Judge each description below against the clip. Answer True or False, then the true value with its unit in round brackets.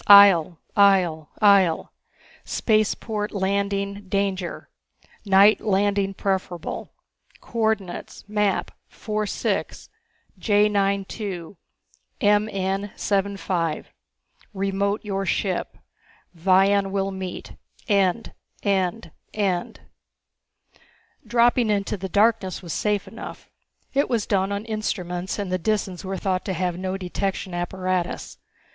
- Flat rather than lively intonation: True (1.7 semitones)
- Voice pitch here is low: False (195 Hz)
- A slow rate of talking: True (95 wpm)